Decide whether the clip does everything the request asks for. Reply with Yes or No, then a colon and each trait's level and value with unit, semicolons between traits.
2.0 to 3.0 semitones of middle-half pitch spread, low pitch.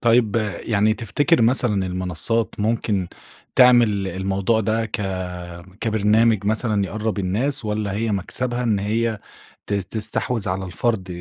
Yes: average, 2.7 semitones; low, 110 Hz